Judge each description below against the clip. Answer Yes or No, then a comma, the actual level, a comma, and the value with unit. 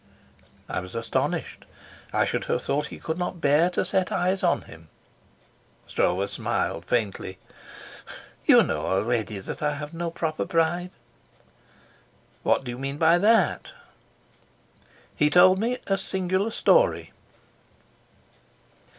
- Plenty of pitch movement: Yes, wide, 7.1 semitones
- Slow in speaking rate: Yes, slow, 125 wpm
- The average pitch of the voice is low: No, medium, 160 Hz